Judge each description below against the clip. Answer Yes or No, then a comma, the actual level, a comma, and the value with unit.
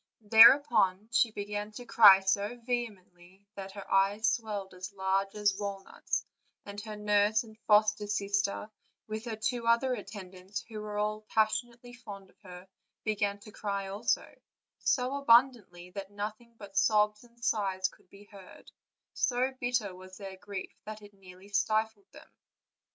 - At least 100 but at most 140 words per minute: No, average, 150 wpm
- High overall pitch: Yes, high, 210 Hz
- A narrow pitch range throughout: Yes, narrow, 2.2 semitones